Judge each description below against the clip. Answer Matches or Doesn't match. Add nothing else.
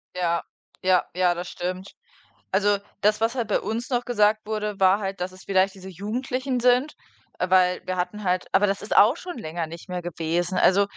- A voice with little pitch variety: Doesn't match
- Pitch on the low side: Doesn't match